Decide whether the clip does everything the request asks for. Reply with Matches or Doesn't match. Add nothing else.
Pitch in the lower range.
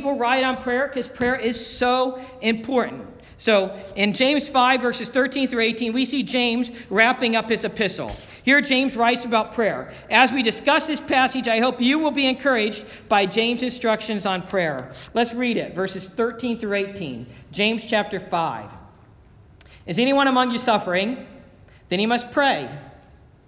Doesn't match